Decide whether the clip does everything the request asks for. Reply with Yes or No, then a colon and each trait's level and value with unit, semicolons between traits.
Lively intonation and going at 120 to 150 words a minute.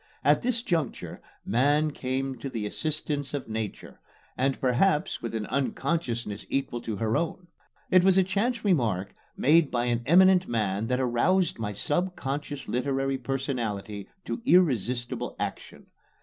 Yes: wide, 6.2 semitones; average, 140 wpm